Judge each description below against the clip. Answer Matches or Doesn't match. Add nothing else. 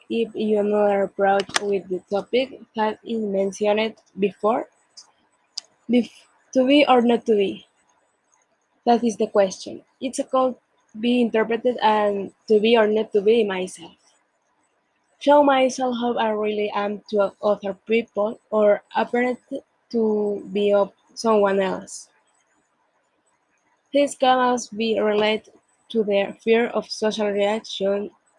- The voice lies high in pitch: Matches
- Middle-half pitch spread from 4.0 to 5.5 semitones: Doesn't match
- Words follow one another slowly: Matches